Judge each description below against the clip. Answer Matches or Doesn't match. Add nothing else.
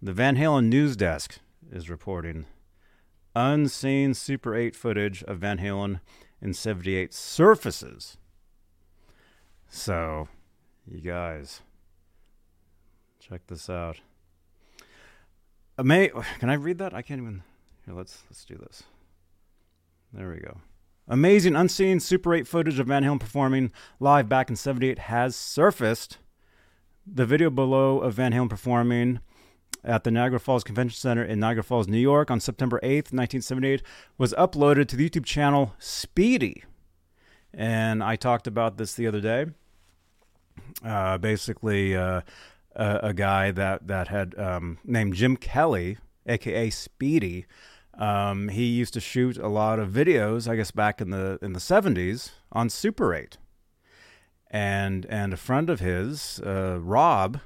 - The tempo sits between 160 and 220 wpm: Doesn't match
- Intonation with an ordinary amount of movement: Doesn't match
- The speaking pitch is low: Matches